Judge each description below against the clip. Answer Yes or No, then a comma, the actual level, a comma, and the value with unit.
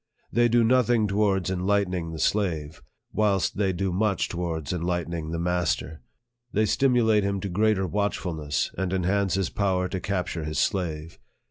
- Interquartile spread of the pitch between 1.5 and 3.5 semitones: Yes, average, 3.1 semitones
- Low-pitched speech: Yes, very low, 95 Hz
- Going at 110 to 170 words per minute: Yes, average, 160 wpm